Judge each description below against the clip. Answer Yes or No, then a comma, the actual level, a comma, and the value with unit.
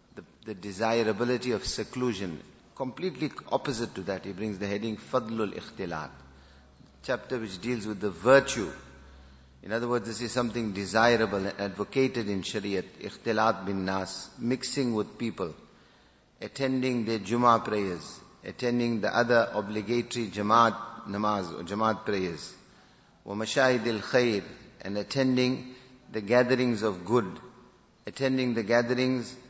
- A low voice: Yes, low, 110 Hz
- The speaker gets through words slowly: Yes, slow, 125 wpm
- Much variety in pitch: No, average, 3.5 semitones